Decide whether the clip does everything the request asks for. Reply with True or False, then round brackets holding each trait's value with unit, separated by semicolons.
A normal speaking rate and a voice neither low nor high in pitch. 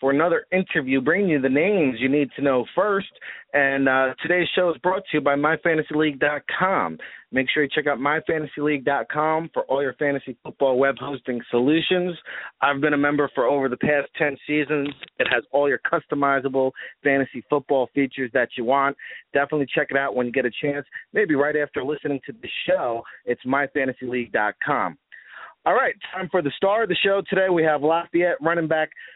True (185 wpm; 145 Hz)